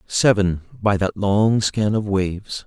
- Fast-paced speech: No, average, 160 wpm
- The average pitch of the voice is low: Yes, low, 100 Hz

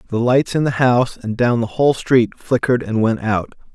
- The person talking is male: Yes, male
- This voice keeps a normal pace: No, fast, 225 wpm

